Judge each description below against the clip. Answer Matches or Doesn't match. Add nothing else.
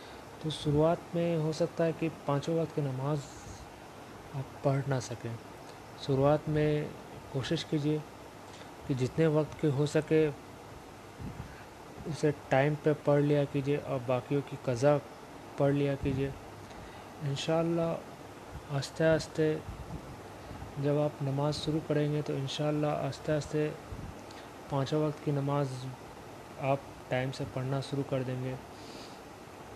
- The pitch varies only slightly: Matches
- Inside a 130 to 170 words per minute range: Doesn't match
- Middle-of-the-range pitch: Matches